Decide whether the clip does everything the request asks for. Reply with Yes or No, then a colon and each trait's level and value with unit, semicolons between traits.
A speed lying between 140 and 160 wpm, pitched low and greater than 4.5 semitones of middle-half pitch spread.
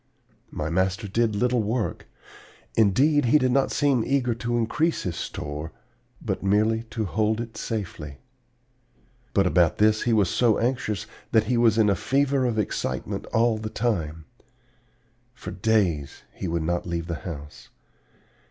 Yes: average, 150 wpm; low, 110 Hz; average, 4.9 semitones